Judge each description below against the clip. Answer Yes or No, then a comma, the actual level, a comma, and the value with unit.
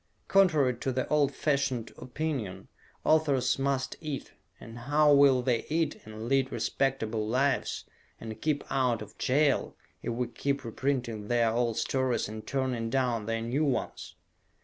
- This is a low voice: Yes, low, 130 Hz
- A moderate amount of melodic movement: Yes, average, 3.3 semitones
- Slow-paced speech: No, average, 150 wpm